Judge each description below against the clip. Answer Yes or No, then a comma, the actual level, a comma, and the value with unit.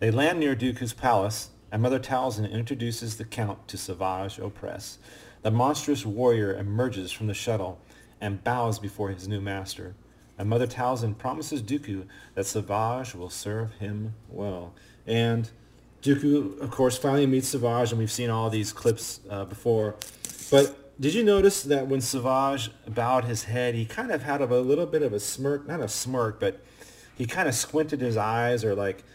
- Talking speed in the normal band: Yes, average, 175 wpm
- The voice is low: Yes, low, 115 Hz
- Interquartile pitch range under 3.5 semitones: No, average, 3.9 semitones